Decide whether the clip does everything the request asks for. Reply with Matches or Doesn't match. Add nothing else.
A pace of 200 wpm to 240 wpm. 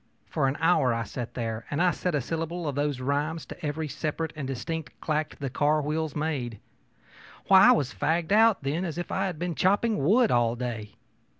Matches